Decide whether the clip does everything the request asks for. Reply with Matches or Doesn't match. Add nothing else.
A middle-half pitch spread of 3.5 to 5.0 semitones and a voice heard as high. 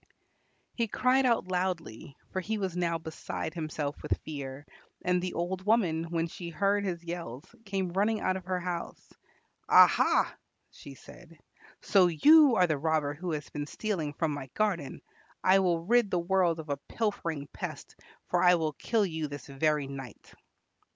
Doesn't match